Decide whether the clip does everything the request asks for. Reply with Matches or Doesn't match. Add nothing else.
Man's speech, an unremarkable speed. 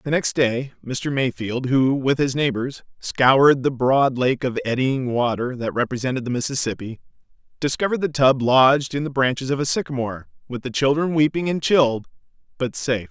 Matches